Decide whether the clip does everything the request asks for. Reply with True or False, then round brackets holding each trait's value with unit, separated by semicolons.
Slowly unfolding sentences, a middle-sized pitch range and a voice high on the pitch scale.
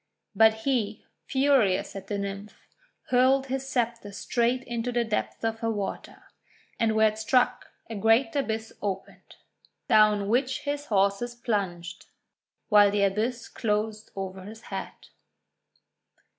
True (130 wpm; 3.1 semitones; 220 Hz)